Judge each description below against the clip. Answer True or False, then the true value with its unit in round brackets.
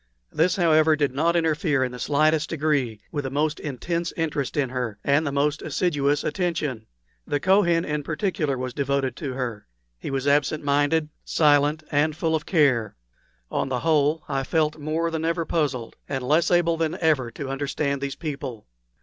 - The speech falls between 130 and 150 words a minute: False (175 wpm)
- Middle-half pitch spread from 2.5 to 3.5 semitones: True (2.9 semitones)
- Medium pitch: True (150 Hz)